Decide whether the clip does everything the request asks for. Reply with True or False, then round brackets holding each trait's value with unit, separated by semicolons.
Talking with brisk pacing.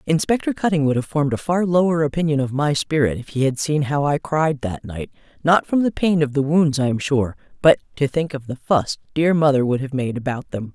True (245 wpm)